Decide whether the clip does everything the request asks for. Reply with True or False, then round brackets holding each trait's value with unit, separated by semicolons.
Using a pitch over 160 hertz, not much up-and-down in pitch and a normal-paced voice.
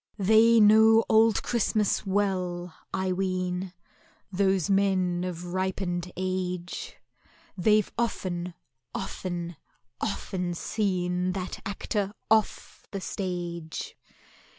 False (185 Hz; 2.2 semitones; 90 wpm)